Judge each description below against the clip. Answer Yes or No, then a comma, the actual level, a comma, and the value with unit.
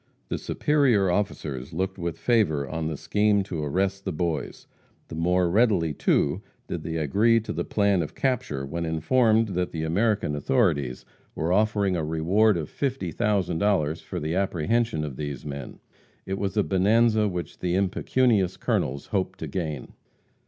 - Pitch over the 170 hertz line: No, very low, 90 Hz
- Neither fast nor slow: Yes, average, 160 wpm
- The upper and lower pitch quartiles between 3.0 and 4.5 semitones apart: No, average, 4.9 semitones